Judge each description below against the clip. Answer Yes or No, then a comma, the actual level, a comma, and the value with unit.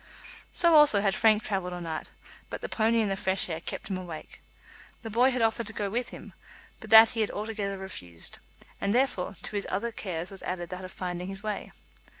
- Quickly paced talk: Yes, fast, 215 wpm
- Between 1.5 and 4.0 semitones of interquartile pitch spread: Yes, average, 3.4 semitones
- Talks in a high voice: Yes, high, 200 Hz